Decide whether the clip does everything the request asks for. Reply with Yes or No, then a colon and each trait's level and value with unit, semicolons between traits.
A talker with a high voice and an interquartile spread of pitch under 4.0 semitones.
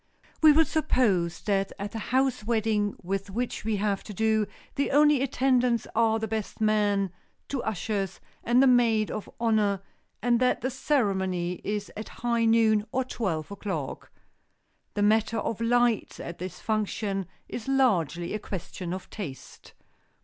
Yes: high, 215 Hz; average, 3.6 semitones